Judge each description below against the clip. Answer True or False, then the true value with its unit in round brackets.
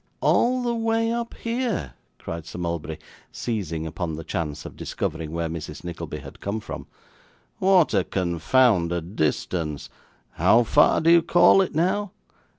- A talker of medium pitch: False (95 Hz)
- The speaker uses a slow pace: False (150 wpm)